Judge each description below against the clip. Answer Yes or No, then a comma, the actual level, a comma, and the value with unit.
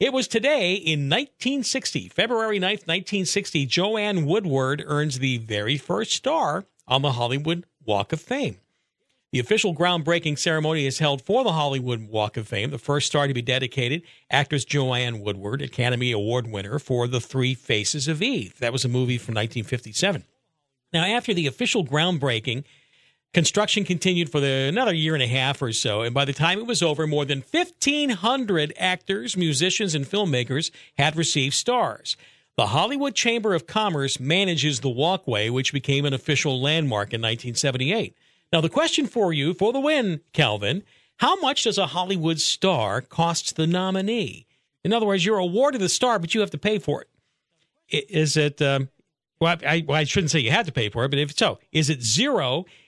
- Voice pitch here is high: No, medium, 155 Hz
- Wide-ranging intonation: Yes, wide, 6.0 semitones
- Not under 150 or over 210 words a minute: Yes, average, 180 wpm